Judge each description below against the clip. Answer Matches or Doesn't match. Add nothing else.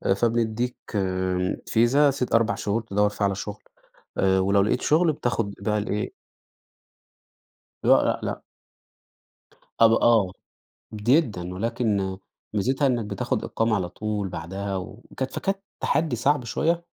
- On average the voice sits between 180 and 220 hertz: Doesn't match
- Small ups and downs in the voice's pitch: Doesn't match